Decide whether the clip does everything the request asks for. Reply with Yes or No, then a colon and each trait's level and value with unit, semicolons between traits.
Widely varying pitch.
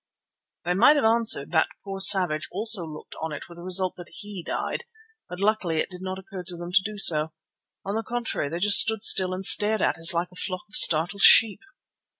No: average, 3.3 semitones